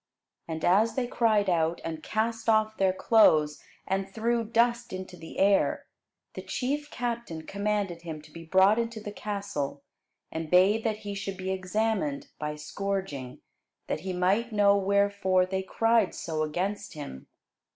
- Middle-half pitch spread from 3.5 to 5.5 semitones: Yes, average, 3.9 semitones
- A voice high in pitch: Yes, high, 200 Hz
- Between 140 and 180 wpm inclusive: Yes, average, 155 wpm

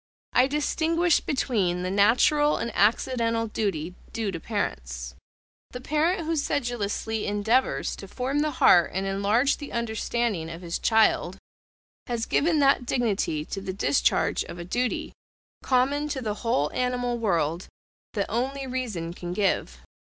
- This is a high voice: Yes, high, 230 Hz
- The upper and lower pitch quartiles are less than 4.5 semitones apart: No, average, 5.1 semitones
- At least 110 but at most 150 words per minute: Yes, average, 145 wpm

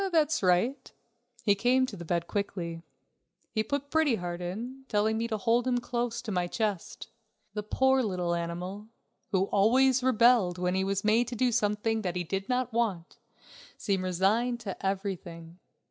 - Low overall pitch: No, high, 210 Hz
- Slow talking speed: No, average, 170 wpm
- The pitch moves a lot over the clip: No, average, 4.9 semitones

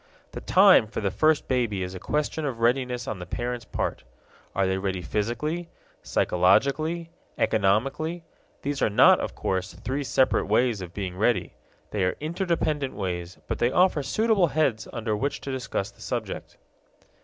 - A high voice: No, low, 120 Hz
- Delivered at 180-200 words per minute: No, average, 165 wpm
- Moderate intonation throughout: No, wide, 7.3 semitones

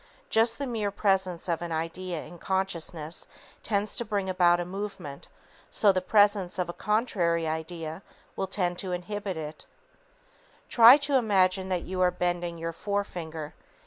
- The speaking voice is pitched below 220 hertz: Yes, medium, 185 Hz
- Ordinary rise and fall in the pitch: Yes, average, 3.1 semitones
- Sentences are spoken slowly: No, average, 160 wpm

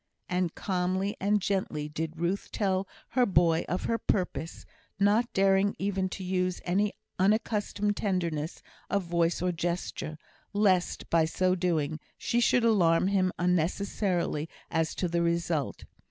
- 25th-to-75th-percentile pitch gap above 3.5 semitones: No, average, 2.9 semitones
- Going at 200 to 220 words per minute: No, average, 140 wpm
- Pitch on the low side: No, medium, 185 Hz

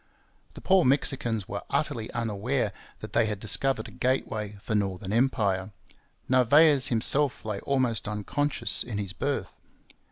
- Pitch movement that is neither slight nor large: Yes, average, 4.4 semitones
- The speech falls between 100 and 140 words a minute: Yes, slow, 135 wpm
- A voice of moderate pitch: No, low, 115 Hz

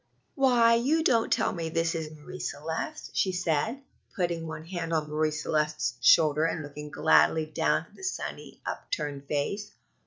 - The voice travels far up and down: No, average, 4.7 semitones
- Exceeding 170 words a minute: No, average, 160 wpm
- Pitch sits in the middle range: Yes, medium, 165 Hz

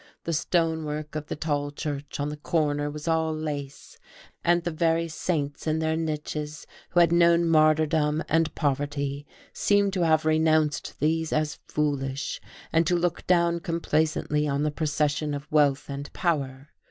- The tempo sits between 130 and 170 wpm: Yes, average, 155 wpm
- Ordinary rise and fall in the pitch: No, narrow, 2.0 semitones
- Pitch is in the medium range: Yes, medium, 155 Hz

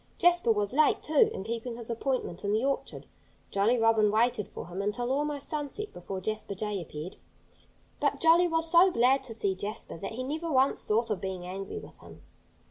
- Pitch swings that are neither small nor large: No, wide, 5.9 semitones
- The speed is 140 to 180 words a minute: No, average, 195 wpm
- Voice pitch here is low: No, high, 230 Hz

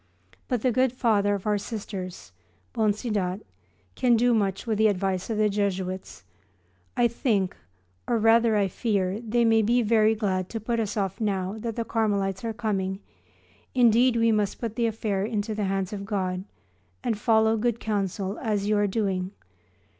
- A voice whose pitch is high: Yes, high, 215 Hz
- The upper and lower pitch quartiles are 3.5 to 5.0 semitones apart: No, average, 2.7 semitones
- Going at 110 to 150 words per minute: No, average, 170 wpm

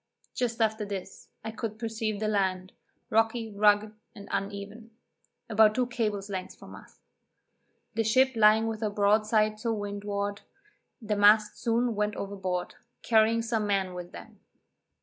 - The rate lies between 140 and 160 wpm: Yes, average, 145 wpm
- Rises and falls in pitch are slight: Yes, narrow, 1.7 semitones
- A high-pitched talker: Yes, high, 215 Hz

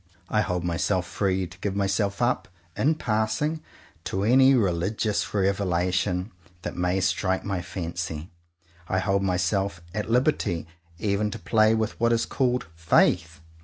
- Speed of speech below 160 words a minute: Yes, average, 140 wpm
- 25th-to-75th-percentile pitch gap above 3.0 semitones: Yes, average, 3.4 semitones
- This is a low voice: Yes, low, 100 Hz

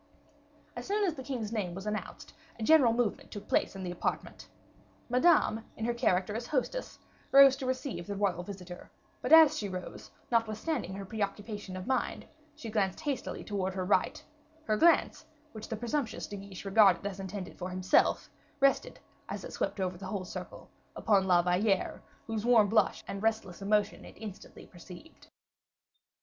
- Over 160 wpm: Yes, average, 170 wpm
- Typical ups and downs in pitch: Yes, average, 3.9 semitones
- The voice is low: No, high, 210 Hz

